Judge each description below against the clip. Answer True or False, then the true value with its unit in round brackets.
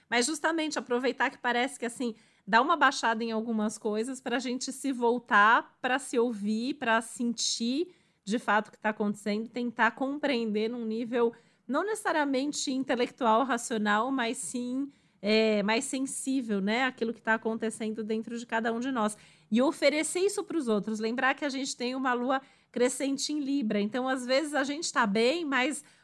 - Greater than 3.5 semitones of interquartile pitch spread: False (3.2 semitones)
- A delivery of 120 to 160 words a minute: False (175 wpm)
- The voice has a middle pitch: False (245 Hz)